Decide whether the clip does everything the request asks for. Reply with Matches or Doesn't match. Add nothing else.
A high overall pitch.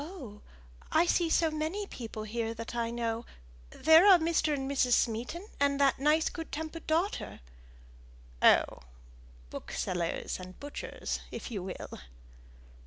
Matches